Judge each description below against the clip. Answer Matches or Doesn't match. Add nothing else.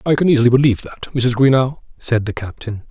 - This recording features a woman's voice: Doesn't match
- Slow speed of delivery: Doesn't match